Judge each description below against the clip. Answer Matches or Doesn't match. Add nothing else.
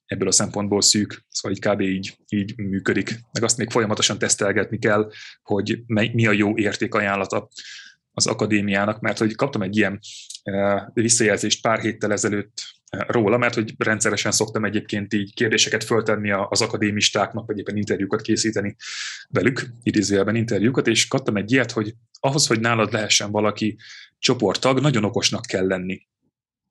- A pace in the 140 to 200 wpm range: Matches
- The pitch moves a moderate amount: Doesn't match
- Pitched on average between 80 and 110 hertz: Matches